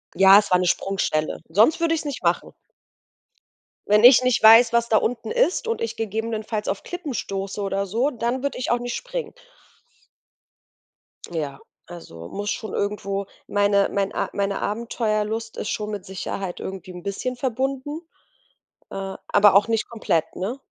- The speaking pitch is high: Yes, high, 215 Hz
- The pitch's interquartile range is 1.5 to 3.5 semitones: No, average, 3.9 semitones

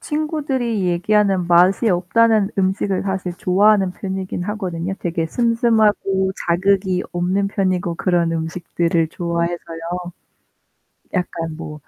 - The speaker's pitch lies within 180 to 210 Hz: Yes, medium, 185 Hz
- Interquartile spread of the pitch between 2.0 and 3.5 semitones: Yes, average, 2.9 semitones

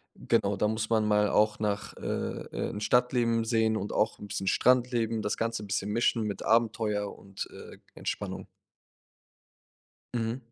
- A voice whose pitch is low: Yes, low, 110 Hz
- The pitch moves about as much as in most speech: No, narrow, 1.8 semitones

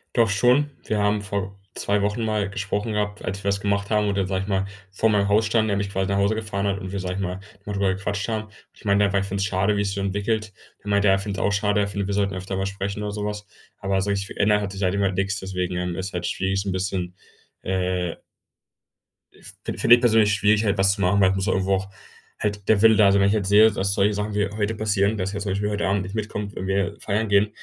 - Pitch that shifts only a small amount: Yes, narrow, 1.2 semitones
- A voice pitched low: Yes, low, 100 Hz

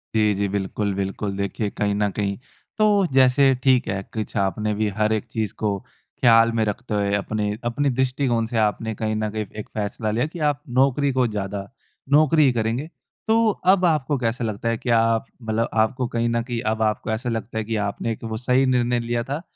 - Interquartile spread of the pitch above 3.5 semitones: No, average, 3.1 semitones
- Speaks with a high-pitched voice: No, low, 115 Hz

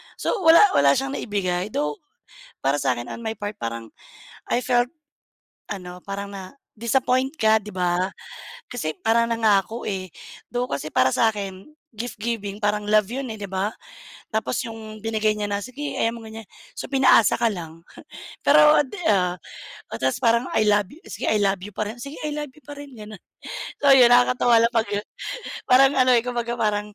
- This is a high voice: Yes, high, 220 Hz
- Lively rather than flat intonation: No, average, 3.7 semitones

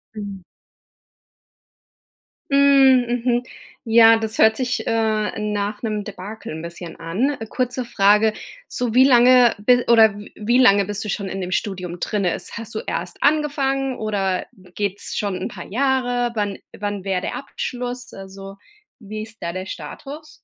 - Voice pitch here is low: No, high, 215 Hz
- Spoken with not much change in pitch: No, average, 3.8 semitones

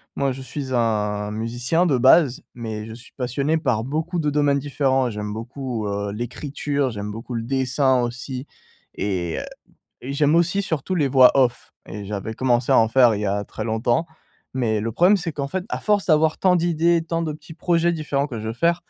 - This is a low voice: Yes, low, 130 Hz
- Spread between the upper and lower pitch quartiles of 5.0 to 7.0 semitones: Yes, wide, 5.4 semitones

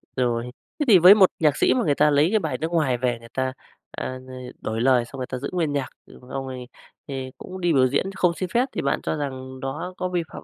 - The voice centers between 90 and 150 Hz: Yes, medium, 140 Hz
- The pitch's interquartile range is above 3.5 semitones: Yes, average, 5.3 semitones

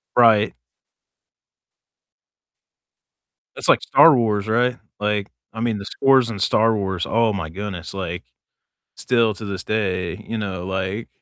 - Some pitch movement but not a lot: Yes, average, 3.0 semitones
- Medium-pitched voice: No, low, 105 Hz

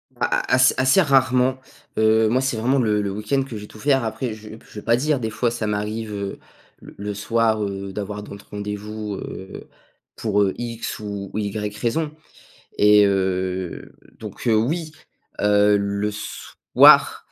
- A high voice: No, low, 105 Hz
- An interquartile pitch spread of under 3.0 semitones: Yes, narrow, 2.6 semitones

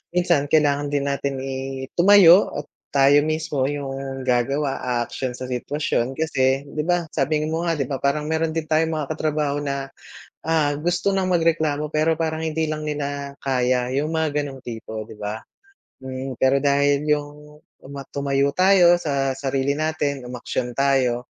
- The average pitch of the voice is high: No, medium, 140 Hz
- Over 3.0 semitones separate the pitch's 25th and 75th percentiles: No, average, 2.7 semitones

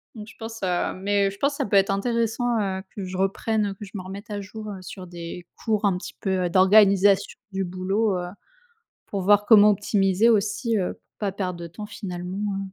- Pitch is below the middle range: No, high, 195 Hz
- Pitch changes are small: Yes, narrow, 2.2 semitones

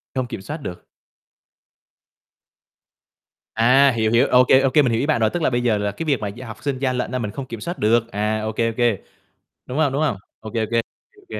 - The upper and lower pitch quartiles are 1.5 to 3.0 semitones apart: No, average, 3.6 semitones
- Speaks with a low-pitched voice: Yes, low, 120 Hz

